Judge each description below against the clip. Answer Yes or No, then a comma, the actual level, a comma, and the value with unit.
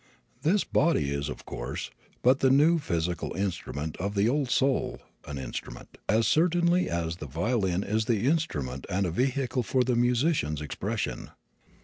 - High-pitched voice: No, low, 110 Hz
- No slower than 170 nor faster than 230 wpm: No, average, 155 wpm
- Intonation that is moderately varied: No, wide, 8.6 semitones